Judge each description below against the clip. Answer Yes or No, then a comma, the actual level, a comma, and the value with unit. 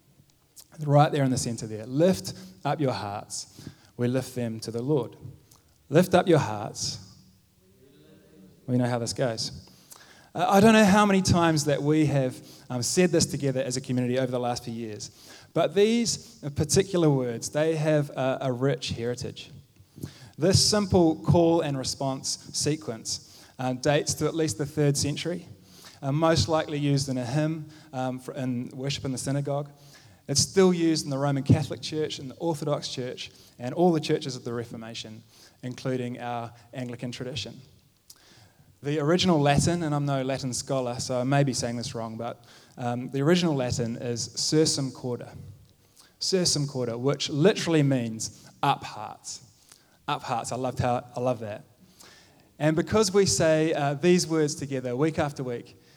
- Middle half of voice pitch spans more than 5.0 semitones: No, average, 4.0 semitones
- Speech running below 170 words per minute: Yes, average, 160 wpm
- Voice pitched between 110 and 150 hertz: Yes, medium, 140 Hz